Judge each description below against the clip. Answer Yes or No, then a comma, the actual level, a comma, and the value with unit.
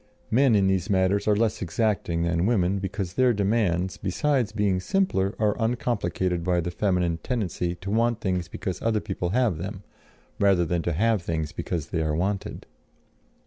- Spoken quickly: No, average, 170 wpm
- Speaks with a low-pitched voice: Yes, very low, 95 Hz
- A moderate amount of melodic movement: Yes, average, 3.7 semitones